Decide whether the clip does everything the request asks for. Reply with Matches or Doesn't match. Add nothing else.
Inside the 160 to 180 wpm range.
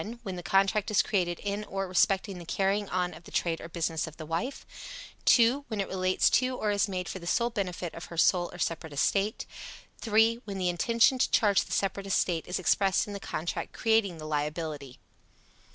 Doesn't match